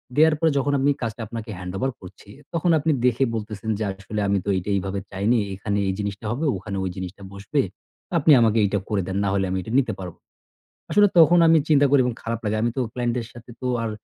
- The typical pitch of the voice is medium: No, low, 110 Hz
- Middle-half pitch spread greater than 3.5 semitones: Yes, average, 4.9 semitones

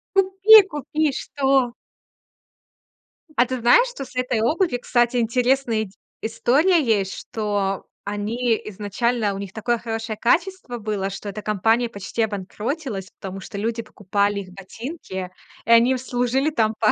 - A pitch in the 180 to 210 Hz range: No, high, 230 Hz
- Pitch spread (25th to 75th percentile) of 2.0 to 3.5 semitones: No, average, 3.9 semitones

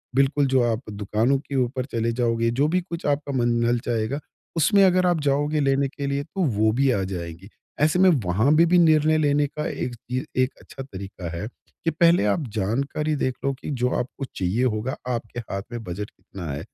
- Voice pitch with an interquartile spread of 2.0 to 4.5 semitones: No, average, 5.0 semitones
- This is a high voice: No, low, 130 Hz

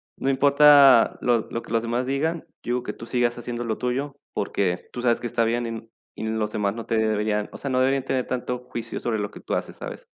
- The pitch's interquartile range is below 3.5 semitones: Yes, narrow, 2.6 semitones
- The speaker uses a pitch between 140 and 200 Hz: No, low, 120 Hz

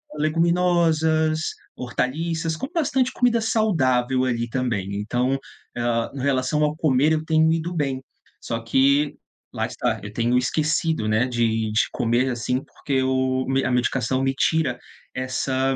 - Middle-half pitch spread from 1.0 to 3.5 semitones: No, average, 4.3 semitones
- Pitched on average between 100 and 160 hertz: Yes, low, 135 Hz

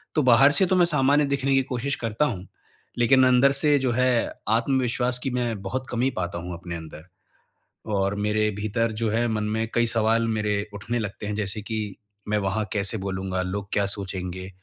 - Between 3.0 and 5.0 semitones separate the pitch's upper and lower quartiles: Yes, average, 4.0 semitones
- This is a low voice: Yes, low, 110 Hz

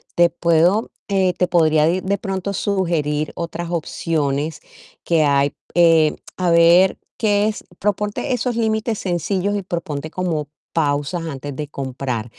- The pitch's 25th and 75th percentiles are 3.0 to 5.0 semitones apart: Yes, average, 4.1 semitones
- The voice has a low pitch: No, medium, 170 Hz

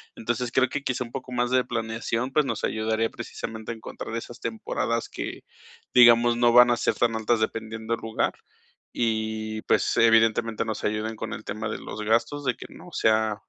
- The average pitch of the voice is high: No, low, 115 Hz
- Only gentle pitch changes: Yes, narrow, 1.6 semitones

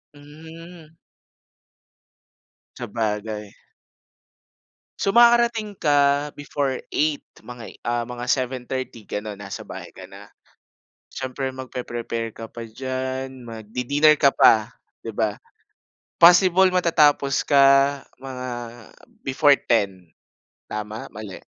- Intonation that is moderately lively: Yes, average, 4.4 semitones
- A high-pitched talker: No, low, 130 Hz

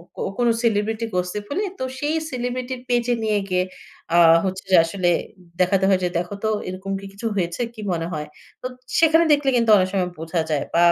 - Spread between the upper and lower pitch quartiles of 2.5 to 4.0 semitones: No, average, 5.1 semitones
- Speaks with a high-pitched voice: Yes, high, 200 Hz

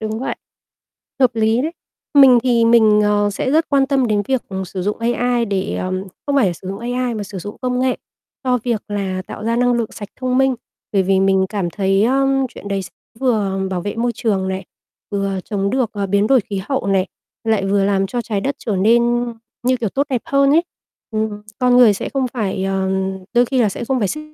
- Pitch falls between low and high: No, high, 220 Hz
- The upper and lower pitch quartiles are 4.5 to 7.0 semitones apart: No, average, 4.1 semitones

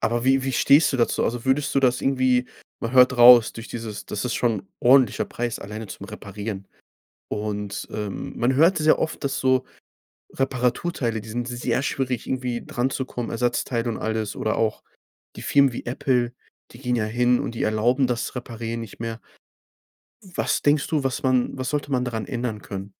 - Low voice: Yes, low, 120 Hz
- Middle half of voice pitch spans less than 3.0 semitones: Yes, narrow, 2.6 semitones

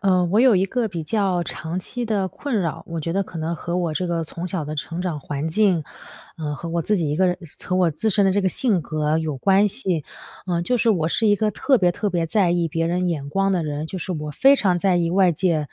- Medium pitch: Yes, medium, 180 Hz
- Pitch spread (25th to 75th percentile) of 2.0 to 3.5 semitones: Yes, average, 3.2 semitones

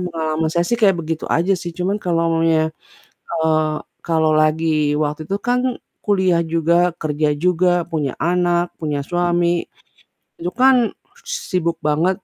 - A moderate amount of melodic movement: No, narrow, 2.3 semitones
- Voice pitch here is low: No, medium, 170 Hz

